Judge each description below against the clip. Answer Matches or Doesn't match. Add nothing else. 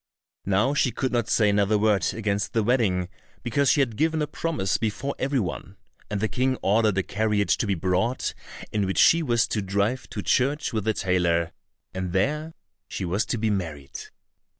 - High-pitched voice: Doesn't match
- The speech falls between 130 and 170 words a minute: Doesn't match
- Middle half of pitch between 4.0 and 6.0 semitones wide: Matches